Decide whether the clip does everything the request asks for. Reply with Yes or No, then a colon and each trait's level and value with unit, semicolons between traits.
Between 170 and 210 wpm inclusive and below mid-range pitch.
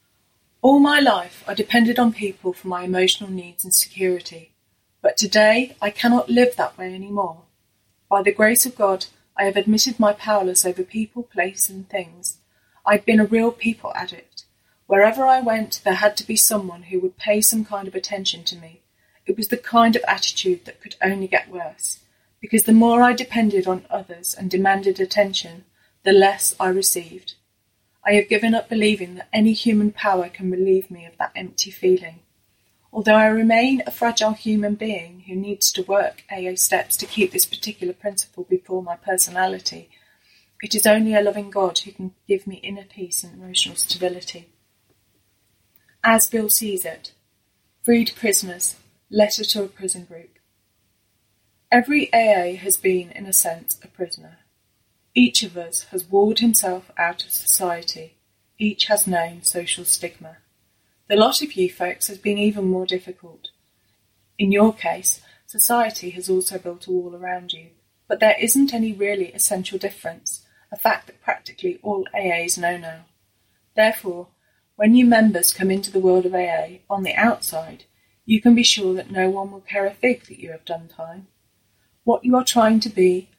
No: average, 175 wpm; high, 190 Hz